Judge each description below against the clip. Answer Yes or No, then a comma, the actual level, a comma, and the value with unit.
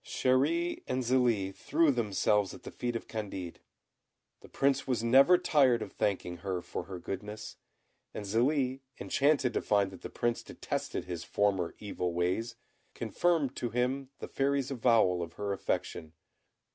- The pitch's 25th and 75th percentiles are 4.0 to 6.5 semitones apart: Yes, average, 5.3 semitones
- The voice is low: Yes, low, 115 Hz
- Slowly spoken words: No, average, 155 wpm